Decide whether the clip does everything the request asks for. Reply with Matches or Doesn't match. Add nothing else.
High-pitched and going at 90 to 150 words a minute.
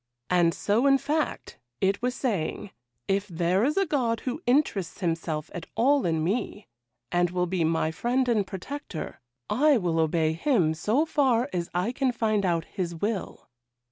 Doesn't match